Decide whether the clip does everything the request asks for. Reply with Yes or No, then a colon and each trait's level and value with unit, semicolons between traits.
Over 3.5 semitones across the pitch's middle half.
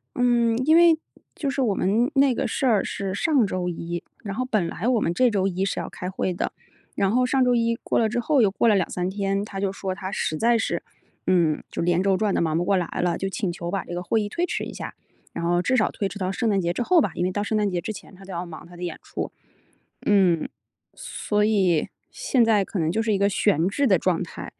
Yes: average, 4.3 semitones